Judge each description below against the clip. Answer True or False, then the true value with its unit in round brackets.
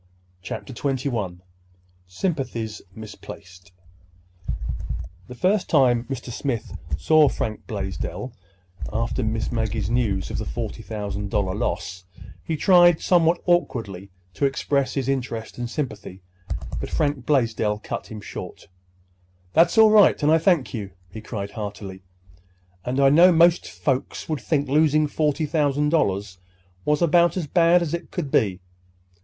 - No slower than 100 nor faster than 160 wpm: True (140 wpm)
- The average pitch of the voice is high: False (130 Hz)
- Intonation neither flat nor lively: False (6.6 semitones)